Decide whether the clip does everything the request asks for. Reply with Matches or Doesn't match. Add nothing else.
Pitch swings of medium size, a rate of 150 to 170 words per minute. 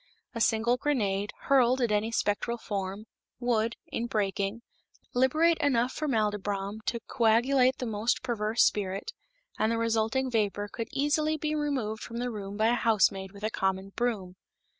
Matches